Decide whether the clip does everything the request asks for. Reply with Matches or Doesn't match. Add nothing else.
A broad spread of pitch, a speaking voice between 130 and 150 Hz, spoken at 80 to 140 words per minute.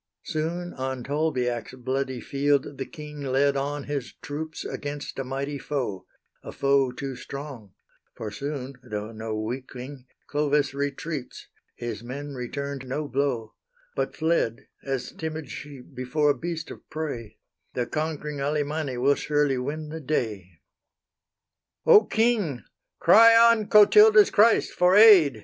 Doesn't match